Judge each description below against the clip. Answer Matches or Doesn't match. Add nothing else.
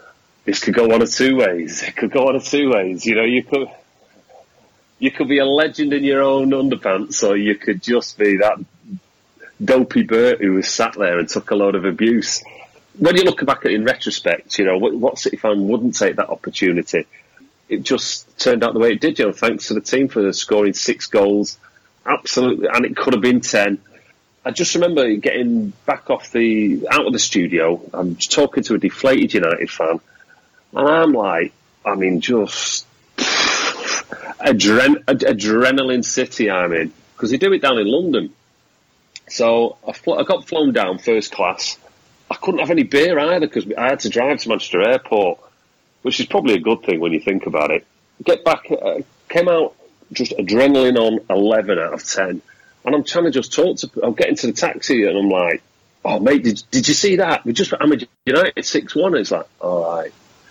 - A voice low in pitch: Matches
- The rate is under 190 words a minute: Doesn't match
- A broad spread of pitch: Matches